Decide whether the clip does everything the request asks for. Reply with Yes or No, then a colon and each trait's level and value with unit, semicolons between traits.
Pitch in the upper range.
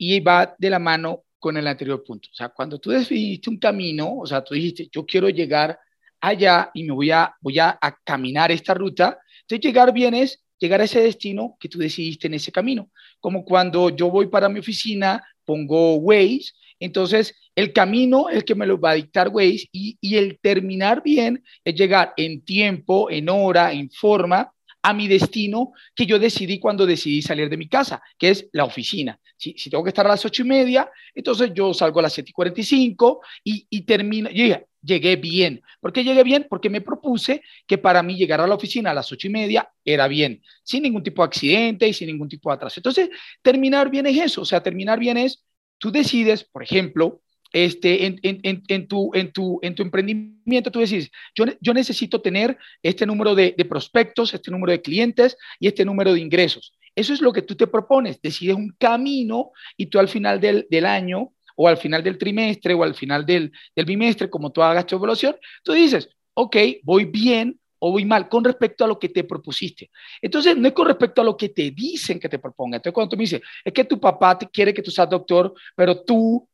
Yes: high, 195 Hz